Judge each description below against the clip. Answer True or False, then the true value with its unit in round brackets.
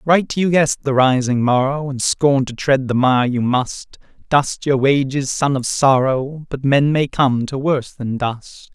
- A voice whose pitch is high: False (135 Hz)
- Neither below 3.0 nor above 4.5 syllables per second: True (4.2 syllables/s)